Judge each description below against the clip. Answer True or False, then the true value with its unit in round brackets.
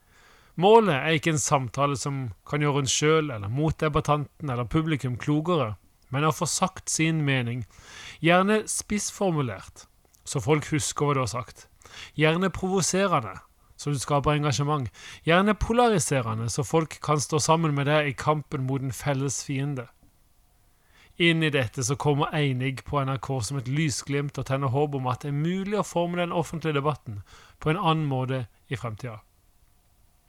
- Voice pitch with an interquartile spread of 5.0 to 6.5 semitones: False (4.0 semitones)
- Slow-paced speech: False (160 wpm)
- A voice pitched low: False (145 Hz)